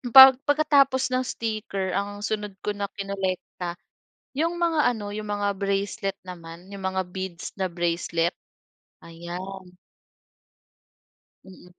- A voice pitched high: Yes, high, 200 Hz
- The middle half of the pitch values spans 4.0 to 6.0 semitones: No, average, 2.9 semitones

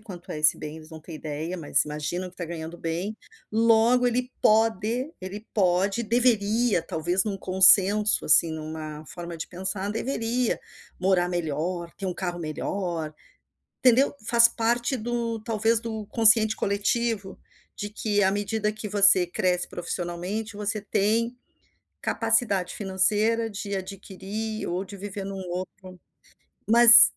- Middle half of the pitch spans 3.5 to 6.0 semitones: Yes, average, 3.9 semitones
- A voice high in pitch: Yes, high, 200 Hz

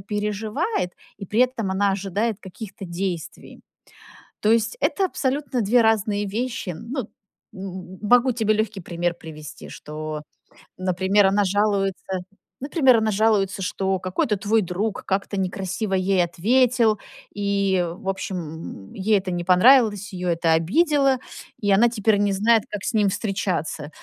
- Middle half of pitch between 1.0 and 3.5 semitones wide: Yes, average, 3.1 semitones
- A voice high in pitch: Yes, high, 200 Hz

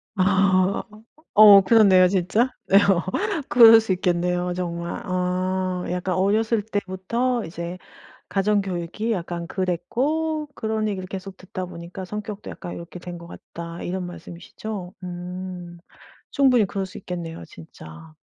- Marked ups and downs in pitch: No, average, 2.9 semitones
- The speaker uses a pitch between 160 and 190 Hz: Yes, medium, 185 Hz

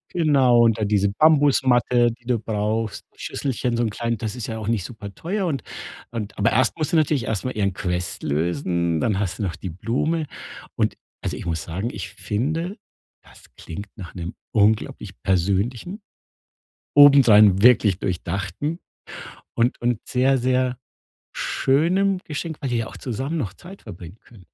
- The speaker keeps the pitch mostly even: No, average, 5.3 semitones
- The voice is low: Yes, low, 115 Hz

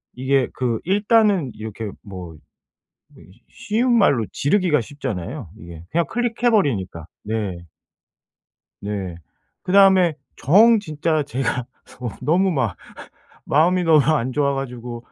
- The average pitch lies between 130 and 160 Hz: Yes, medium, 140 Hz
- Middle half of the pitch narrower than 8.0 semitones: No, wide, 8.4 semitones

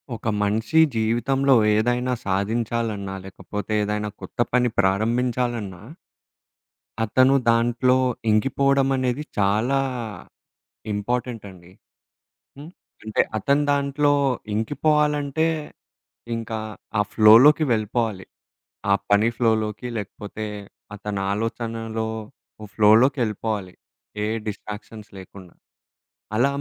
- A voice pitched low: Yes, low, 115 Hz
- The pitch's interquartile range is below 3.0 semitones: No, average, 3.3 semitones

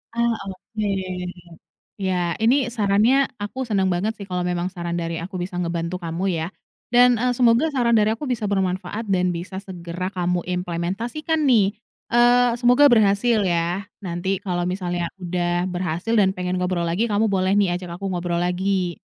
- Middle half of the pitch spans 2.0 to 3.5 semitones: No, average, 4.0 semitones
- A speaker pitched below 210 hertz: Yes, high, 190 Hz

